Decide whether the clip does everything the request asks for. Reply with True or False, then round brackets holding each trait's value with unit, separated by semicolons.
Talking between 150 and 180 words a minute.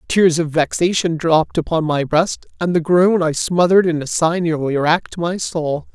False (190 wpm)